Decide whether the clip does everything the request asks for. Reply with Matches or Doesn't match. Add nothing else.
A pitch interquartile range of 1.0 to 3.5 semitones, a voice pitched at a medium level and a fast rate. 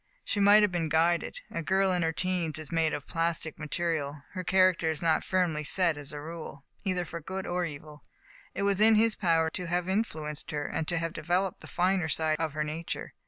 Matches